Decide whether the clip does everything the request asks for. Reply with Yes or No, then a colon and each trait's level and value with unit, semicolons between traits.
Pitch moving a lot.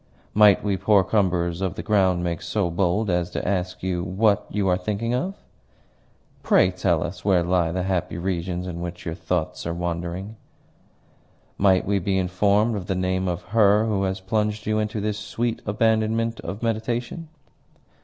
No: average, 3.0 semitones